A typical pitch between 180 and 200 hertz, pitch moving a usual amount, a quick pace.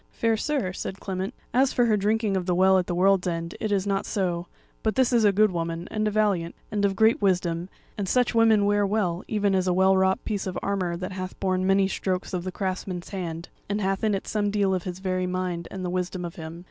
No: high, 190 Hz; narrow, 2.2 semitones; fast, 250 wpm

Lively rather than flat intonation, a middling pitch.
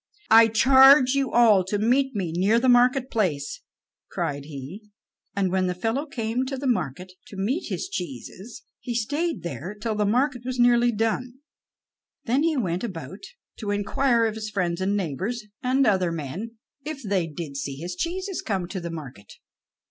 No: wide, 5.7 semitones; high, 215 Hz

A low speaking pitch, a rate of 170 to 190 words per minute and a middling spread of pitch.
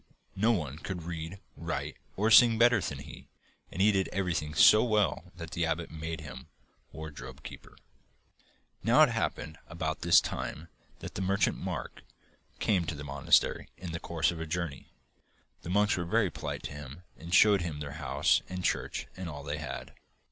Yes: very low, 85 Hz; average, 180 wpm; average, 3.7 semitones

